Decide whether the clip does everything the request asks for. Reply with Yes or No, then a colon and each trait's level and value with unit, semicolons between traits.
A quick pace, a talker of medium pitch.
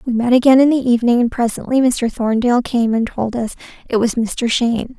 No: fast, 215 wpm; high, 240 Hz